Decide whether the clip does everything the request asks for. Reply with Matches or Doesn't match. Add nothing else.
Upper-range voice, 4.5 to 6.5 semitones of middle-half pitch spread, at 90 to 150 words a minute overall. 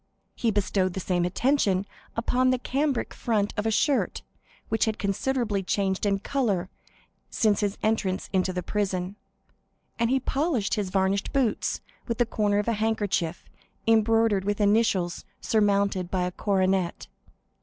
Doesn't match